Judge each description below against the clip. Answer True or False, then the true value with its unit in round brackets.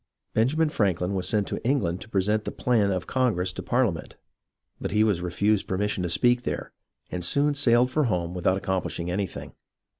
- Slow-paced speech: False (185 wpm)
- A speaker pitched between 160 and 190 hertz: False (100 Hz)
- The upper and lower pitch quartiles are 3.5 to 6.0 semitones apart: True (5.1 semitones)